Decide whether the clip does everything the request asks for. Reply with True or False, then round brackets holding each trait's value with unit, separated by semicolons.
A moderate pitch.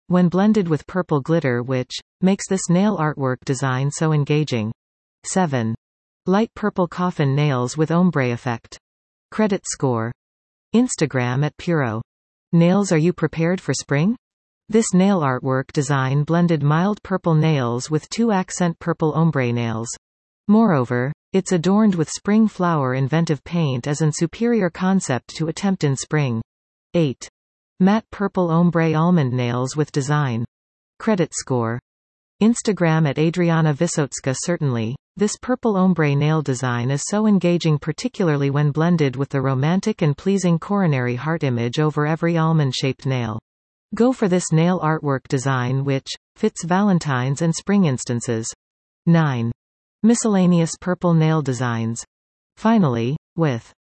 True (155 Hz)